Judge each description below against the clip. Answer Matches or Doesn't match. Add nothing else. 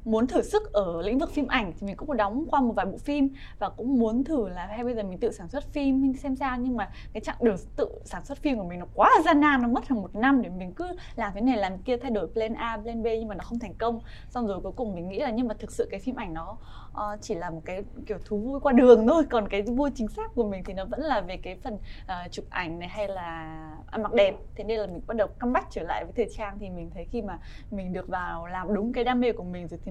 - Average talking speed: Doesn't match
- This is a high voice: Matches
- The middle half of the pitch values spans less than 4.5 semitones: Doesn't match